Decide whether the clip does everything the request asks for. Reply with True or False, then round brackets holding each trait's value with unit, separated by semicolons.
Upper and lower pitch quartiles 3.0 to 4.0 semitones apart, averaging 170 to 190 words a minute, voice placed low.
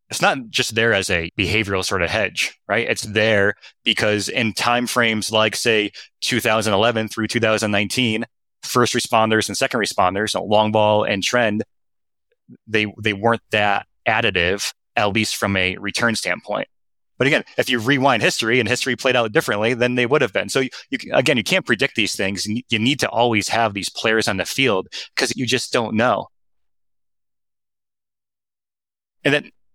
False (2.5 semitones; 175 wpm; 110 Hz)